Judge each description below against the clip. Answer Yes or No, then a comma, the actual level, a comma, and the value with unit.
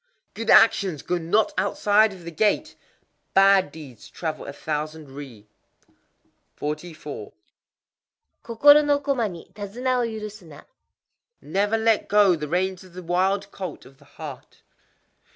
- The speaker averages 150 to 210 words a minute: No, slow, 135 wpm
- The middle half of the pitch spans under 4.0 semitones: No, wide, 5.6 semitones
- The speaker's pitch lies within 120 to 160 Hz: No, medium, 185 Hz